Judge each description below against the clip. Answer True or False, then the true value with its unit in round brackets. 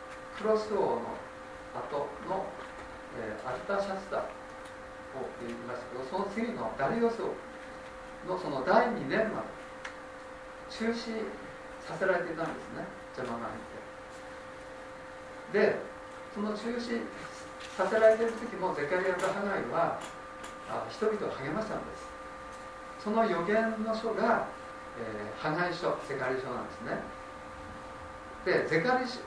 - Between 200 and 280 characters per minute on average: True (240 characters per minute)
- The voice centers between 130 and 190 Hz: False (75 Hz)